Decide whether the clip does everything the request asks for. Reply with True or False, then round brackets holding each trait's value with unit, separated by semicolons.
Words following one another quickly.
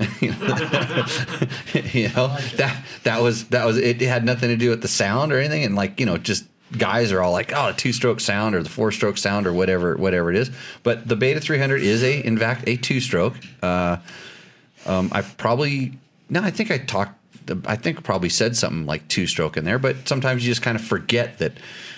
True (215 wpm)